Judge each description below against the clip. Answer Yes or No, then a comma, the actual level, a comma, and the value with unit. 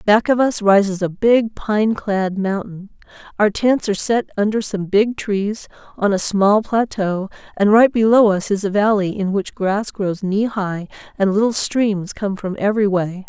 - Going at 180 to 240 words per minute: Yes, average, 185 wpm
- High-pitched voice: Yes, high, 205 Hz